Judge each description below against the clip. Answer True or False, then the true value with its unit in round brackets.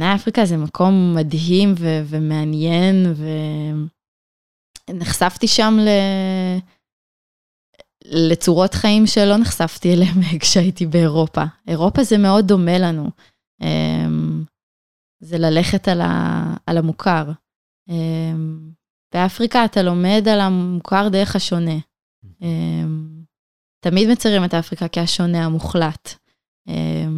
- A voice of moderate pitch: True (170 Hz)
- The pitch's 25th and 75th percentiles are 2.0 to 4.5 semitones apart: True (3.4 semitones)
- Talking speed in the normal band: False (90 wpm)